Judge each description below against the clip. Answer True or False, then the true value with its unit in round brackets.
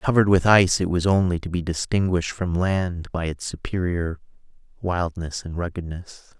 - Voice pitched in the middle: False (90 Hz)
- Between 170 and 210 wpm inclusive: False (160 wpm)